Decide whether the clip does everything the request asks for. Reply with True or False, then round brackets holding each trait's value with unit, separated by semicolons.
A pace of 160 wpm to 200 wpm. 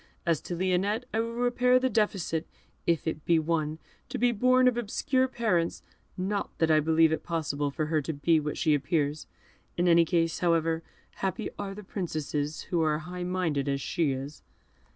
True (190 wpm)